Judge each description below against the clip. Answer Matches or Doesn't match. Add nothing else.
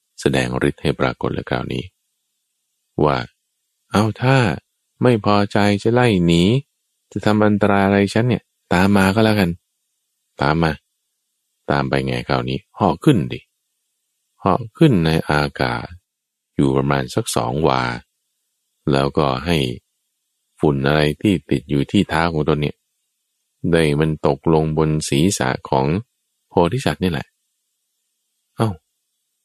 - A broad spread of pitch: Matches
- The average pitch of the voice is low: Matches